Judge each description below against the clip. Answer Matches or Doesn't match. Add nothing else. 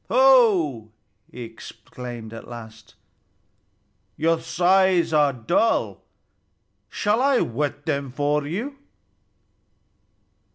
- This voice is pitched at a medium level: Matches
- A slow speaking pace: Matches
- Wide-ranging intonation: Matches